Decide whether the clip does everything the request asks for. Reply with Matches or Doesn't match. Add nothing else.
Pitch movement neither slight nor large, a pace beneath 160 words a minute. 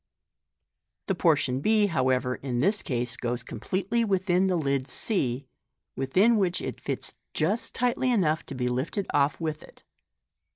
Doesn't match